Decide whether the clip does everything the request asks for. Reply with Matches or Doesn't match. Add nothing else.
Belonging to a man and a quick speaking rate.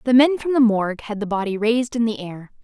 Doesn't match